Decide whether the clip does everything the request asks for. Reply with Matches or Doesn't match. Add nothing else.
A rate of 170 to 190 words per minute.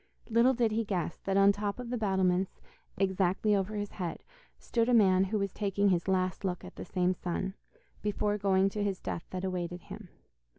Doesn't match